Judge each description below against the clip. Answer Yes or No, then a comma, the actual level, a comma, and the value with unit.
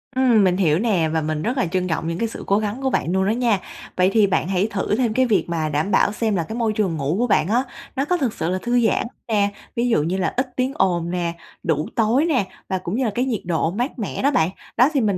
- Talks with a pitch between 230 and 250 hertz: No, high, 205 Hz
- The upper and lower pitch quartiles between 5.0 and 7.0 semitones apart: Yes, wide, 5.6 semitones